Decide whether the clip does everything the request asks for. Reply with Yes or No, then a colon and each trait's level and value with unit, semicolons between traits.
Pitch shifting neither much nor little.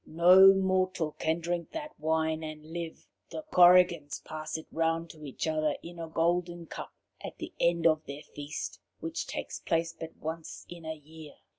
No: narrow, 1.7 semitones